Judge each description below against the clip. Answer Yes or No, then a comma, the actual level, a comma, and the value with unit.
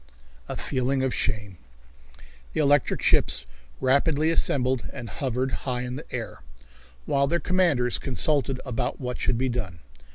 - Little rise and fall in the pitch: Yes, narrow, 2.2 semitones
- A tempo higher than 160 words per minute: No, average, 140 wpm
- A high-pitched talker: No, low, 130 Hz